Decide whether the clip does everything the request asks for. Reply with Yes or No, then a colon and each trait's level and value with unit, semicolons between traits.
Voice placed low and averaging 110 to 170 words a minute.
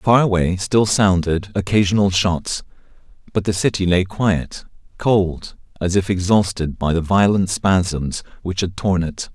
Yes: very low, 95 Hz; average, 150 wpm